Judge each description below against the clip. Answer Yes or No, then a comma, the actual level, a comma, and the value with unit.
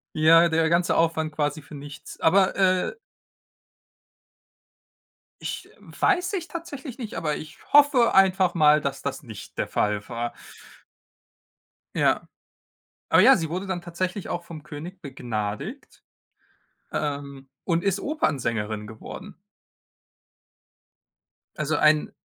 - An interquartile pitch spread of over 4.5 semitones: Yes, average, 5.2 semitones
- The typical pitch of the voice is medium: Yes, medium, 160 Hz